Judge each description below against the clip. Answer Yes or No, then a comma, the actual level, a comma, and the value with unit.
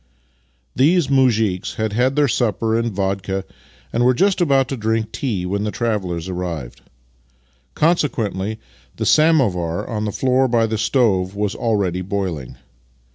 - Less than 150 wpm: Yes, average, 140 wpm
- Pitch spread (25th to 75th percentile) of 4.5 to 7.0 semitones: Yes, average, 5.0 semitones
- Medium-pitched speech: No, low, 110 Hz